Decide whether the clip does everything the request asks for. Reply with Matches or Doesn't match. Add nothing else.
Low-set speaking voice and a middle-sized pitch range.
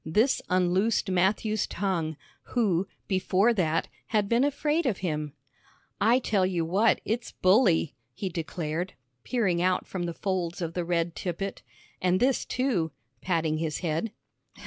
Doesn't match